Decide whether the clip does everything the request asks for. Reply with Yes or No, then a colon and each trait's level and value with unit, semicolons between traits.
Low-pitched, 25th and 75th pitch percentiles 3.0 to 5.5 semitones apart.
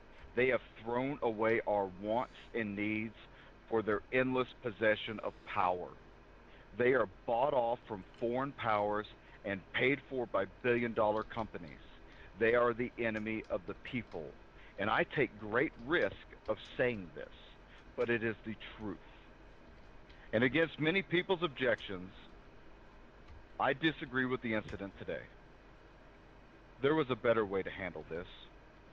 Yes: low, 115 Hz; average, 3.4 semitones